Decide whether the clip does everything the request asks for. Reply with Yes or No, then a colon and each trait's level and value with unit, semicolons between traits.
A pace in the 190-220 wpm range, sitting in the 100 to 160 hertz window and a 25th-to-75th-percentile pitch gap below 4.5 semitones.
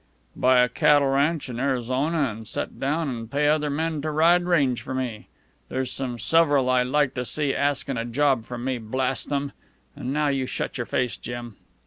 Yes: average, 195 wpm; low, 135 Hz; average, 2.9 semitones